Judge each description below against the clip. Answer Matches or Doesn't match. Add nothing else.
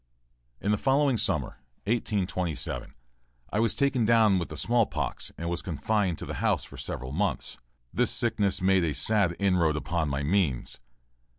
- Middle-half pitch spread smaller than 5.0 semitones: Doesn't match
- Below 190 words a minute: Matches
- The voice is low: Matches